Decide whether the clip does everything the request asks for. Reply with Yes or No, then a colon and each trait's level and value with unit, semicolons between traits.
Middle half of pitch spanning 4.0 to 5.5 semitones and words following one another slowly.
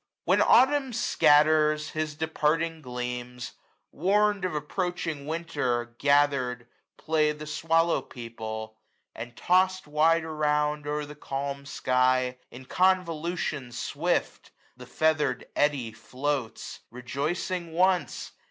Yes: average, 4.4 semitones; slow, 105 wpm